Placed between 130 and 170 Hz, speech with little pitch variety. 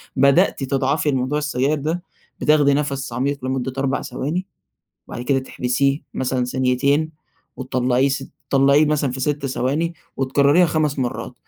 Yes: low, 135 Hz; narrow, 2.1 semitones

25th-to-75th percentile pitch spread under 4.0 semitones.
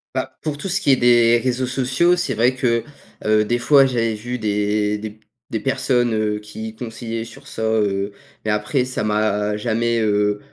Yes: average, 2.9 semitones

